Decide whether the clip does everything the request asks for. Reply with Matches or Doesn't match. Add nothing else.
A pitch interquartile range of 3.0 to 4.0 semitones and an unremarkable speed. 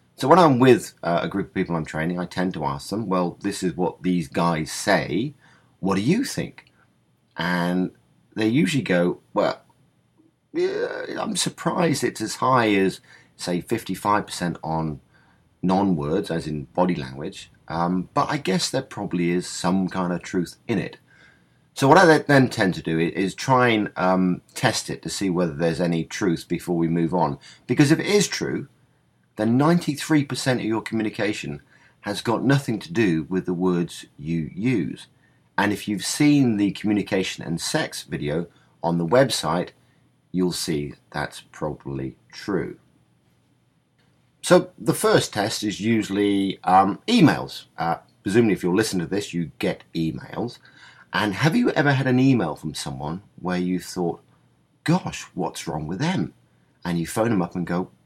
Doesn't match